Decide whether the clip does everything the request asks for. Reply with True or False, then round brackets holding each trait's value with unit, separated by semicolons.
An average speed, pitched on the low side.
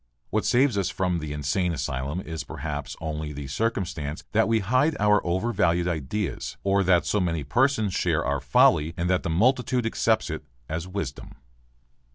True (170 wpm; 90 Hz)